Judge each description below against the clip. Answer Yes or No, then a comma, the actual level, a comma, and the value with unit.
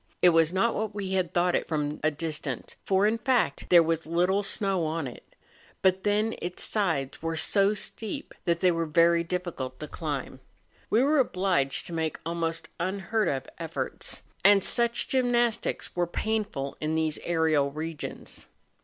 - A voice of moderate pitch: Yes, medium, 175 Hz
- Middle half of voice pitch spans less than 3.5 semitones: No, average, 4.2 semitones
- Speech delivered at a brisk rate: No, average, 170 wpm